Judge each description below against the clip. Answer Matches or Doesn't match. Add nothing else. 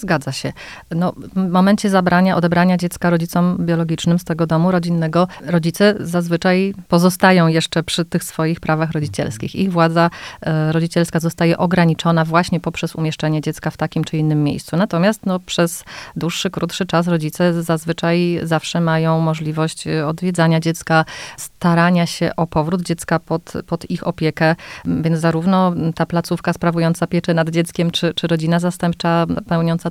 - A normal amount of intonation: Doesn't match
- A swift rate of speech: Doesn't match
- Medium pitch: Matches